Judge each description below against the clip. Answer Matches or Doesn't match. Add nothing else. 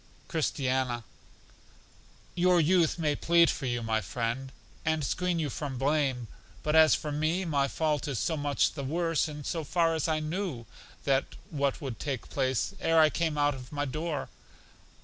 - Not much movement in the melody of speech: Doesn't match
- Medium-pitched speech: Matches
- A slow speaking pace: Doesn't match